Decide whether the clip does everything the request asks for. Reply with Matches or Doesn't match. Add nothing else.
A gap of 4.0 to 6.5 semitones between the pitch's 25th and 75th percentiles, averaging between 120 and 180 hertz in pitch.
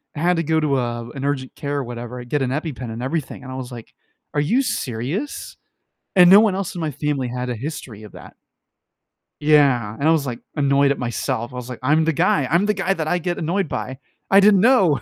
Matches